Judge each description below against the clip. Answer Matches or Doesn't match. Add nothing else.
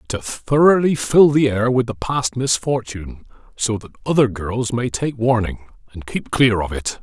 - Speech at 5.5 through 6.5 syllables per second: Doesn't match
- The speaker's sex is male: Matches